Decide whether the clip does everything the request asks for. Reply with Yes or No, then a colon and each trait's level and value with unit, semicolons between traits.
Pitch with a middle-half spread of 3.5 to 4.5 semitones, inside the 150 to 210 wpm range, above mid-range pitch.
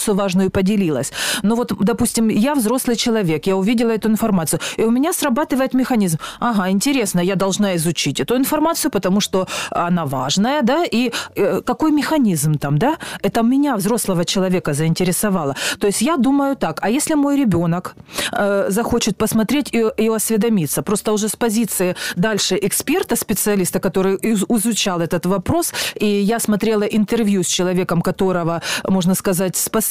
Yes: average, 4.0 semitones; fast, 155 wpm; high, 210 Hz